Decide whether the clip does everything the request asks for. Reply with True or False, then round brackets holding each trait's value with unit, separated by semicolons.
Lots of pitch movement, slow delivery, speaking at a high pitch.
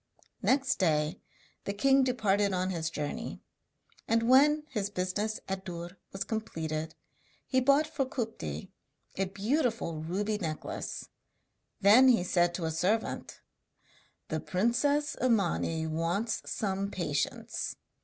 True (5.7 semitones; 120 wpm; 200 Hz)